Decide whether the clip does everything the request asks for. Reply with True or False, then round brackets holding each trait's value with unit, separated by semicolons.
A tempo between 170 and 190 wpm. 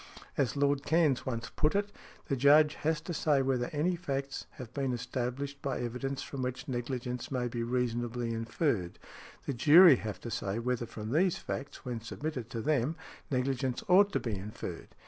True (175 wpm)